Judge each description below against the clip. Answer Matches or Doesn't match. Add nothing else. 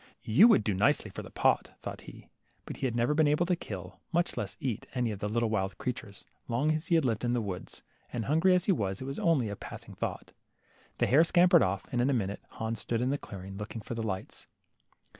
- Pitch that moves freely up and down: Matches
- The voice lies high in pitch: Doesn't match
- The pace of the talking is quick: Matches